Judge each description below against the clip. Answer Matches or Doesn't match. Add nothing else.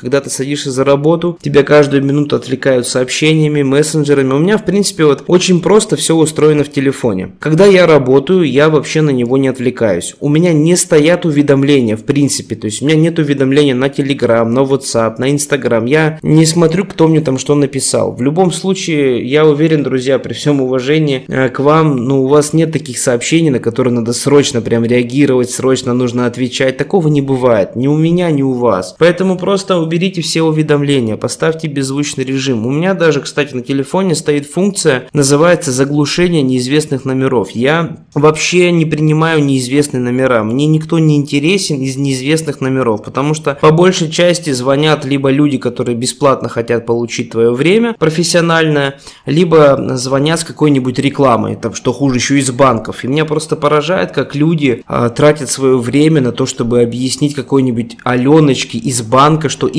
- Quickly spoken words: Matches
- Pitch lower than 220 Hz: Matches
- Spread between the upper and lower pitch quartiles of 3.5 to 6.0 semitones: Doesn't match